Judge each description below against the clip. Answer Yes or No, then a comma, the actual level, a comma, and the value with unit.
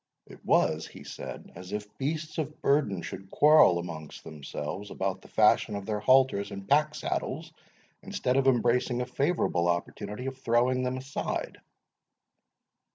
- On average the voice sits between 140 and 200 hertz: No, low, 120 Hz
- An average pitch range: No, wide, 5.8 semitones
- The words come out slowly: No, average, 150 wpm